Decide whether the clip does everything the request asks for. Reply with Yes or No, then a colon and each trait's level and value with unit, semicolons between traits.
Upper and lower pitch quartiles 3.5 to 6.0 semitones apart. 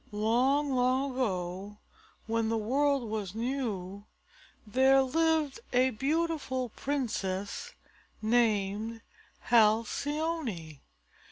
Yes: average, 4.5 semitones